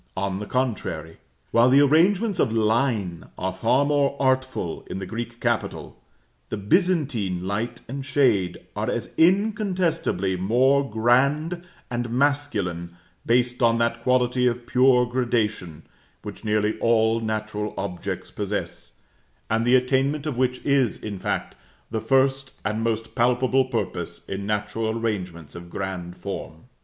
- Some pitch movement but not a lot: Yes, average, 4.3 semitones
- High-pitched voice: No, low, 120 Hz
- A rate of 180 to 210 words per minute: No, slow, 135 wpm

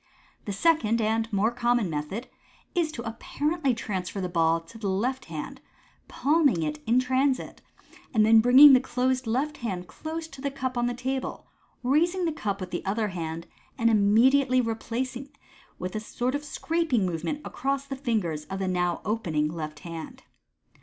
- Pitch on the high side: Yes, high, 230 Hz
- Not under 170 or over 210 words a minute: Yes, average, 175 wpm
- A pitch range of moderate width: No, wide, 5.9 semitones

